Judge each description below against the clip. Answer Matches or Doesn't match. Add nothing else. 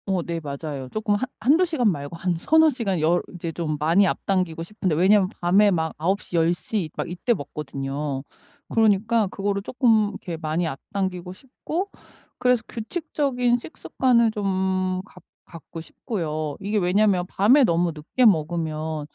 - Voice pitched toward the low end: Doesn't match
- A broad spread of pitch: Doesn't match